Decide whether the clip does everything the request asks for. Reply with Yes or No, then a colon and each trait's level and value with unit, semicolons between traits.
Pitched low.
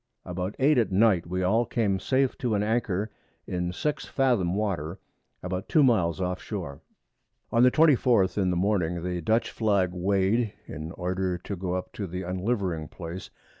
Yes: very low, 95 Hz